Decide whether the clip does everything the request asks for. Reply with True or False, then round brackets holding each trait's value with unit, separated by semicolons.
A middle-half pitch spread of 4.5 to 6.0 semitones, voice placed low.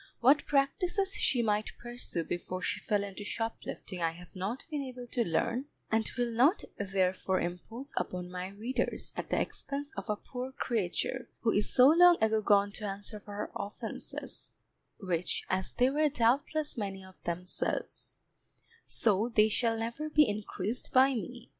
False (4.8 semitones; 225 Hz)